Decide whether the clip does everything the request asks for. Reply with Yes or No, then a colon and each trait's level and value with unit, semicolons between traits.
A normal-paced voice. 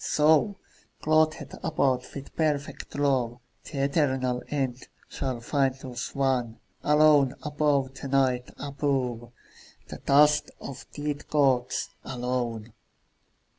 No: slow, 110 wpm